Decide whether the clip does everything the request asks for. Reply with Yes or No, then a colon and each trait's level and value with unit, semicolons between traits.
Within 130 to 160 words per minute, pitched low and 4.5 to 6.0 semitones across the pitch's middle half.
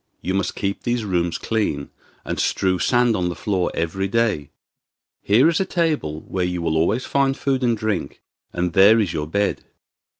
No: average, 180 wpm; low, 100 Hz; average, 5.1 semitones